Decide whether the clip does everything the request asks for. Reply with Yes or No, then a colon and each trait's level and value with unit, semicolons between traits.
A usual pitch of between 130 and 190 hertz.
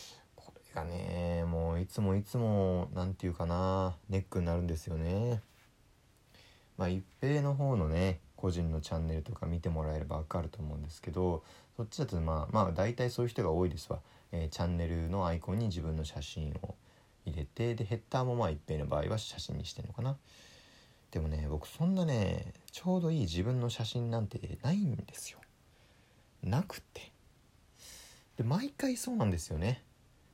No: very low, 95 Hz